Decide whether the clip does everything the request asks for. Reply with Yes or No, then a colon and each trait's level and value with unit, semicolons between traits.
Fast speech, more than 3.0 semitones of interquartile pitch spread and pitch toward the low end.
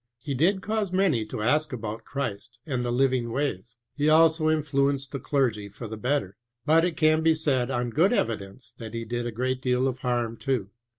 Yes: fast, 210 wpm; average, 4.6 semitones; low, 130 Hz